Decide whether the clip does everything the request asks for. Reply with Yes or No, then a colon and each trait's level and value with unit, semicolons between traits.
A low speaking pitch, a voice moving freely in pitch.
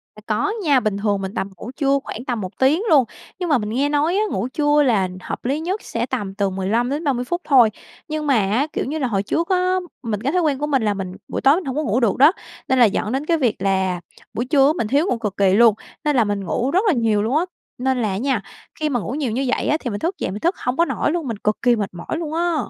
No: very high, 255 Hz; wide, 6.0 semitones